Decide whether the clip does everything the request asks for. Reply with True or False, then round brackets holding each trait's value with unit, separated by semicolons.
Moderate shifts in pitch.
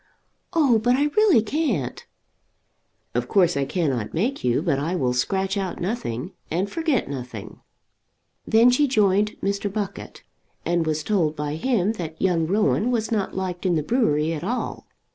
False (6.4 semitones)